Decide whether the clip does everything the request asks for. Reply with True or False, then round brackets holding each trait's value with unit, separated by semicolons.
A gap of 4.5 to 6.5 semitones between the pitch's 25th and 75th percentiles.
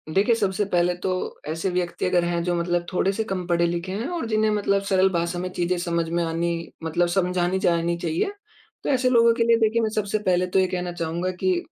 False (3.0 semitones)